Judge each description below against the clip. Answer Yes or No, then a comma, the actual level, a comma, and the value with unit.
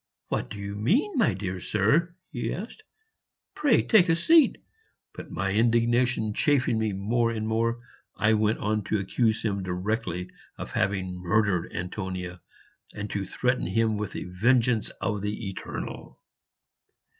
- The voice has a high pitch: No, low, 110 Hz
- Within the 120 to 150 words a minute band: Yes, average, 145 wpm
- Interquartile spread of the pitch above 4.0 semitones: No, average, 3.5 semitones